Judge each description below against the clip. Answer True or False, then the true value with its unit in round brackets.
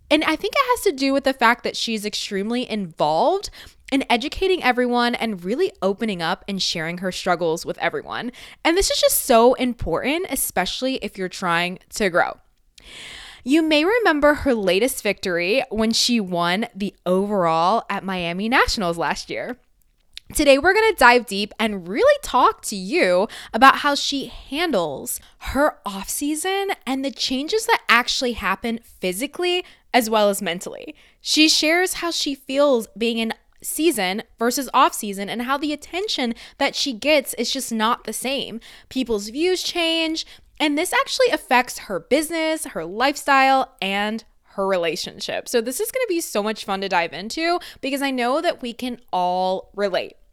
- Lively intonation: True (6.6 semitones)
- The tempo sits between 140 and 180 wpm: True (170 wpm)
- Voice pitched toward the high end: True (245 Hz)